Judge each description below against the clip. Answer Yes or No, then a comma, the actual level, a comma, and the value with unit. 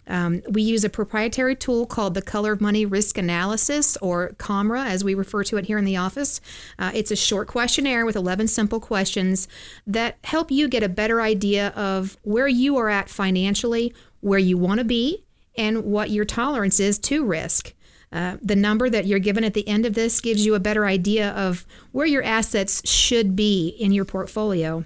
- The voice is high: Yes, high, 210 Hz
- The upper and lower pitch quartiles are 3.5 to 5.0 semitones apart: No, average, 2.7 semitones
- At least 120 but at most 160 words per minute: No, average, 200 wpm